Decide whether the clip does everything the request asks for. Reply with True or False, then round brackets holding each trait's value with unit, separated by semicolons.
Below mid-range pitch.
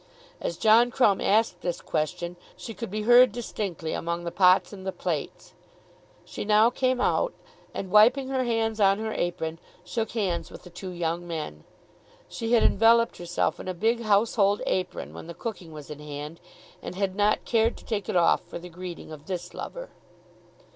False (195 Hz)